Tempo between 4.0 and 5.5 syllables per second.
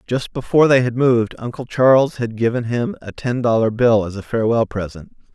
No: 5.7 syllables/s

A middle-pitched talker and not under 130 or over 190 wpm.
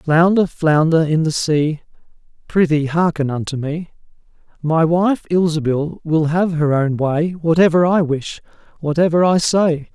Yes: medium, 160 Hz; average, 140 wpm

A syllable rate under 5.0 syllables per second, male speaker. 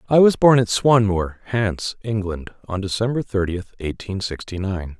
Yes: 4.6 syllables/s; male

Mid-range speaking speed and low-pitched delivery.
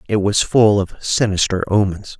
Yes: average, 165 wpm; low, 100 Hz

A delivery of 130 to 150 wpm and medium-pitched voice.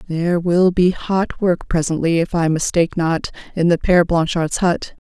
No: average, 175 wpm; medium, 170 Hz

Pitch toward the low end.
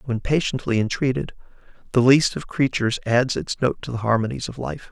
Yes: low, 120 Hz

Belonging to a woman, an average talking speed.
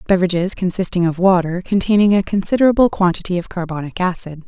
Yes: female; average, 150 wpm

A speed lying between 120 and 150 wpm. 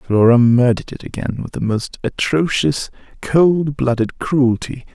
Yes: slow, 135 wpm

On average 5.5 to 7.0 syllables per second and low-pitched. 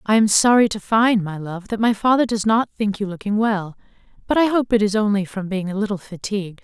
No: 5.7 syllables/s; high, 210 Hz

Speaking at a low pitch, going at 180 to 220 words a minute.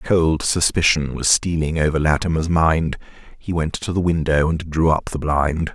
Yes: very low, 80 Hz; average, 190 wpm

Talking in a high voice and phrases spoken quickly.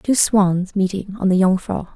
No: high, 195 Hz; average, 185 wpm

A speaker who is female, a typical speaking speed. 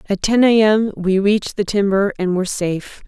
No: female; fast, 215 wpm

